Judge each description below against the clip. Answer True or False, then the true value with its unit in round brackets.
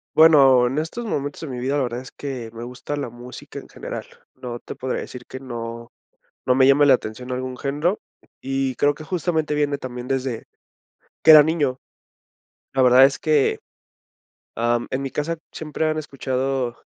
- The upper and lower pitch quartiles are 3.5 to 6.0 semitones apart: False (2.8 semitones)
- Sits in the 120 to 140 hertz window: True (135 Hz)